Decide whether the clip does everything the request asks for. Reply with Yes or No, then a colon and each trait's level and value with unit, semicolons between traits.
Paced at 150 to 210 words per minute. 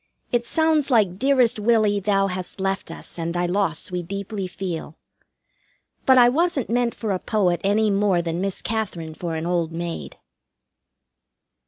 Yes: average, 160 wpm